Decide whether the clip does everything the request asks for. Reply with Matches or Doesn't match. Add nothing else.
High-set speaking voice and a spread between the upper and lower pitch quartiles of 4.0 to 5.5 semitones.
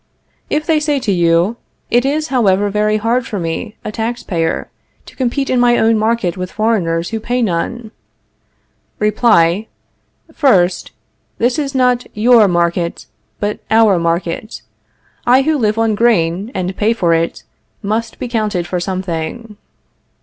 Matches